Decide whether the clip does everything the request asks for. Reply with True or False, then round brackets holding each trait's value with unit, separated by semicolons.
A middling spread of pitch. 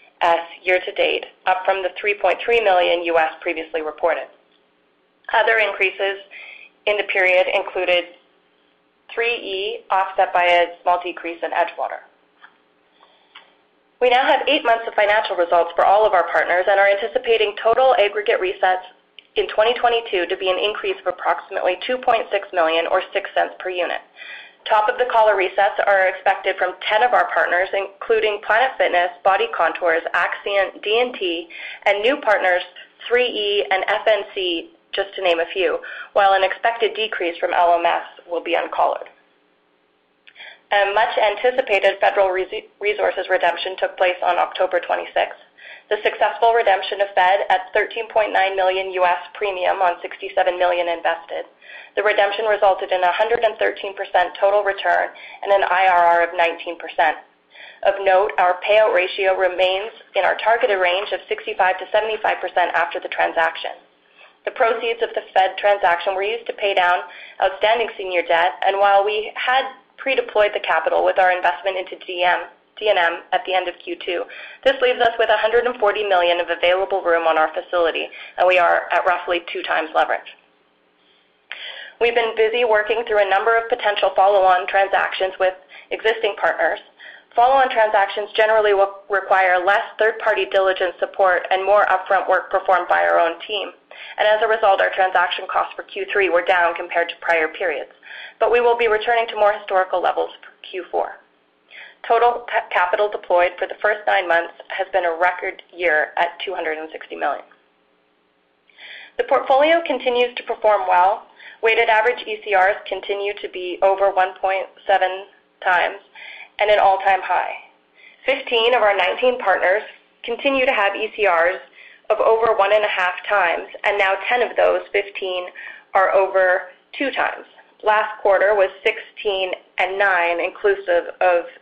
True (3.3 semitones)